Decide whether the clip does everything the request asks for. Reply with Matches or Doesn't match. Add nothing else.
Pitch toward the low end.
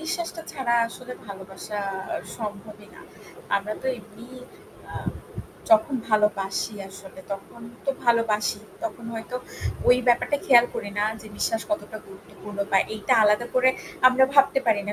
Doesn't match